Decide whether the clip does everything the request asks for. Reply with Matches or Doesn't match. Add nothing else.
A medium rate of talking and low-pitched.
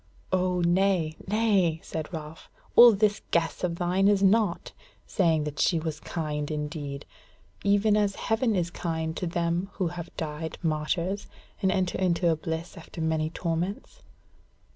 Doesn't match